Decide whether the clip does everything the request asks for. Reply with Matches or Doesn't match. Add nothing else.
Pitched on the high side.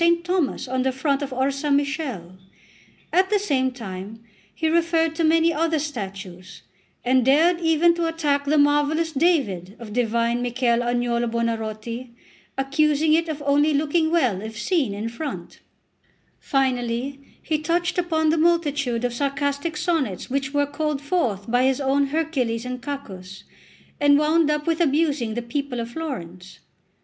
Matches